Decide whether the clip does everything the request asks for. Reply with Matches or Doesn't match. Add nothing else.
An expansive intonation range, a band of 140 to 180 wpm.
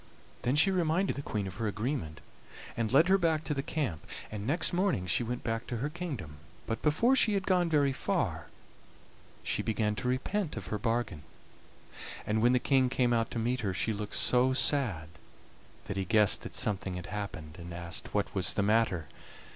Doesn't match